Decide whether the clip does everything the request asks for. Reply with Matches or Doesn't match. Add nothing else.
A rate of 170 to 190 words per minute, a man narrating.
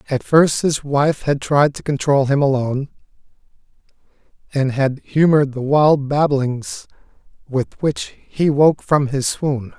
Doesn't match